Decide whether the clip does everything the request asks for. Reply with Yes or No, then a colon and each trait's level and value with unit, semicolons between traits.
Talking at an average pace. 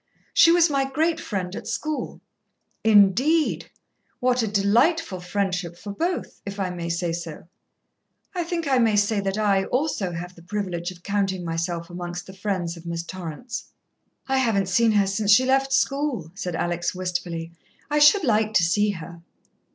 Yes: average, 170 wpm